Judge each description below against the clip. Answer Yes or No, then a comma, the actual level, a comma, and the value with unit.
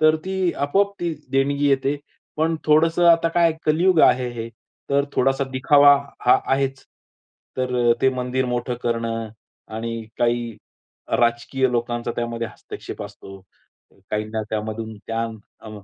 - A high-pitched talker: No, low, 125 Hz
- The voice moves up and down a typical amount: Yes, average, 3.8 semitones